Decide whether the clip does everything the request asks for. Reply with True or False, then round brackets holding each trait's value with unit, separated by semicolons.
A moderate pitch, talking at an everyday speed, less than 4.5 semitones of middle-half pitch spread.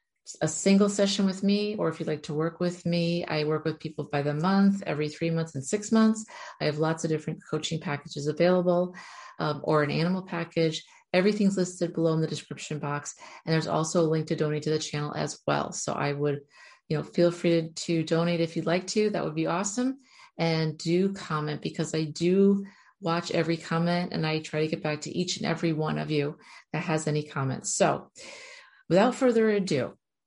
False (165 Hz; 210 wpm; 2.8 semitones)